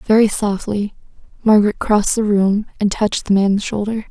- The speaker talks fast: No, average, 160 wpm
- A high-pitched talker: Yes, high, 205 Hz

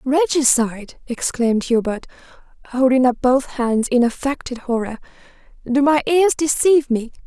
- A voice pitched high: Yes, very high, 260 Hz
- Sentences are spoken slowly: Yes, slow, 125 wpm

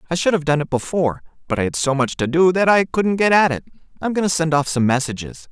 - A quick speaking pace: Yes, fast, 285 wpm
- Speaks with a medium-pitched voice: Yes, medium, 160 Hz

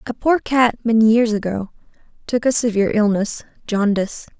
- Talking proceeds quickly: No, slow, 135 wpm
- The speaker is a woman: Yes, female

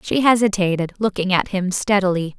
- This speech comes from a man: No, female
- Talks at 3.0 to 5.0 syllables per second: No, 5.4 syllables/s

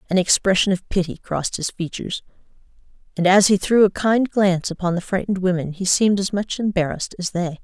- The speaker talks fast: No, average, 195 wpm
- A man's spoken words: No, female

